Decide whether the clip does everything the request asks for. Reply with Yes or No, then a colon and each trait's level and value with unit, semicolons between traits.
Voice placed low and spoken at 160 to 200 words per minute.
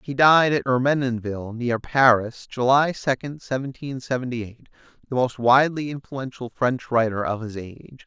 No: low, 125 Hz; average, 150 wpm